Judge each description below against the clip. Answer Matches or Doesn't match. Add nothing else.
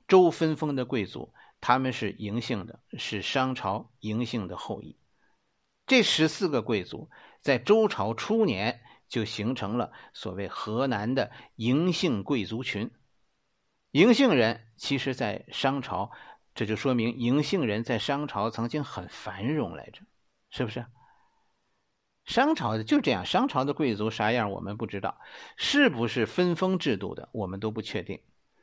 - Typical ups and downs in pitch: Doesn't match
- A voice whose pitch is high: Doesn't match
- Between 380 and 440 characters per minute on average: Doesn't match